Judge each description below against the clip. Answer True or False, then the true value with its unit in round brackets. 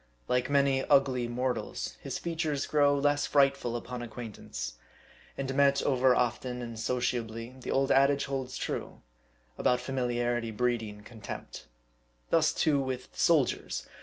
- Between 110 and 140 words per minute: True (135 wpm)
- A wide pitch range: False (2.5 semitones)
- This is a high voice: False (125 Hz)